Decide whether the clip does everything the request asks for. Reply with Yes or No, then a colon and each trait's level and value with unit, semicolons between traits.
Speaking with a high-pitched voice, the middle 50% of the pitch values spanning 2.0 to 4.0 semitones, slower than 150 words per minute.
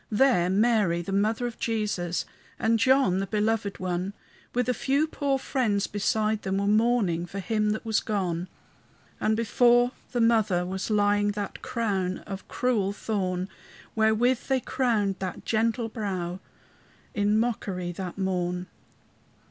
Yes: high, 210 Hz; average, 3.3 semitones; average, 140 wpm